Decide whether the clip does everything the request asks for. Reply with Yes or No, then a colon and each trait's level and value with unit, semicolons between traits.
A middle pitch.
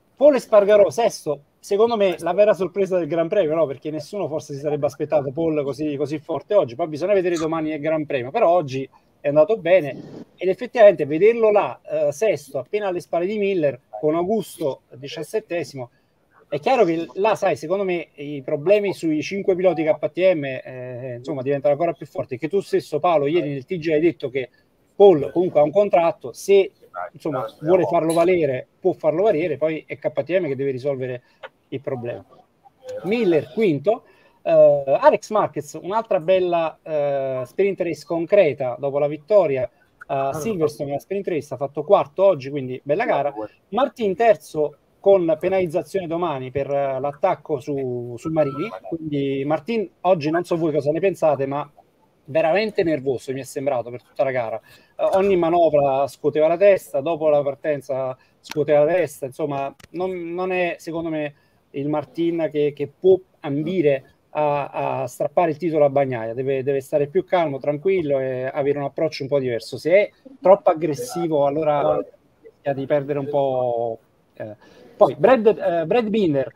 Yes: medium, 155 Hz